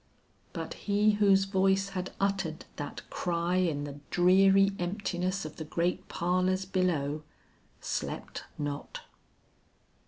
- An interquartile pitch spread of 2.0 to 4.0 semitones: Yes, narrow, 2.5 semitones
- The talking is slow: Yes, slow, 115 wpm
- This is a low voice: No, medium, 185 Hz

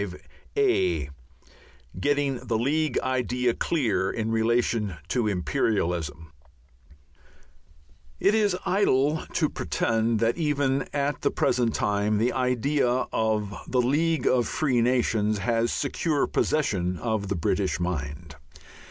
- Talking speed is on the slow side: Yes, slow, 120 wpm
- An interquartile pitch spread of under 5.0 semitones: No, average, 5.3 semitones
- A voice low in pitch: Yes, low, 120 Hz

